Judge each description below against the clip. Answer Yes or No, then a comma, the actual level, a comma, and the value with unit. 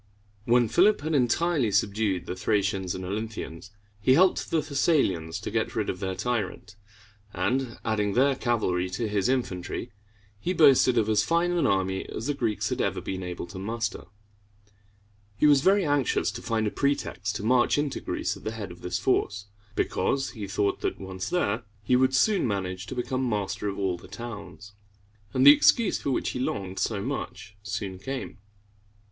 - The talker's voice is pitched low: Yes, low, 110 Hz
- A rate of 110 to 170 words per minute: No, average, 180 wpm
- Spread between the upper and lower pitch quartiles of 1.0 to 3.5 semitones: No, average, 5.3 semitones